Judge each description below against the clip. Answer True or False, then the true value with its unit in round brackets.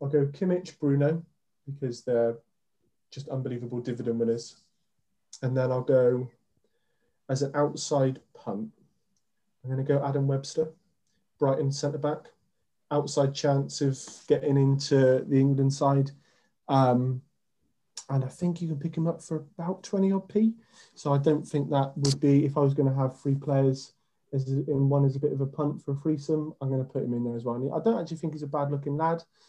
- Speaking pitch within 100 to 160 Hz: True (140 Hz)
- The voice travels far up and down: False (2.5 semitones)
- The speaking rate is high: False (190 wpm)